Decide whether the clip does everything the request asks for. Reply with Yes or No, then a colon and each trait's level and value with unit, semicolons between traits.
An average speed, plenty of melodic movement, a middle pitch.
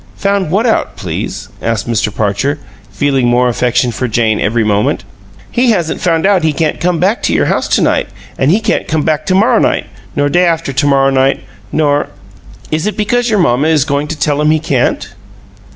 No: fast, 210 wpm; wide, 6.0 semitones; medium, 150 Hz